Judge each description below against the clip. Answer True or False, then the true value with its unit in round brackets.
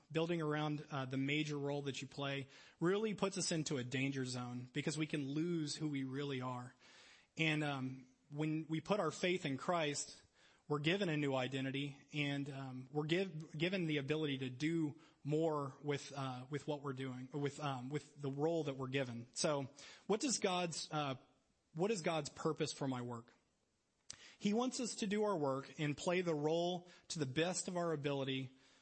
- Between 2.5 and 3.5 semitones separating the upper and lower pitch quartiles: True (3.2 semitones)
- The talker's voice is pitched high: False (150 Hz)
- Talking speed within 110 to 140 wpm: False (190 wpm)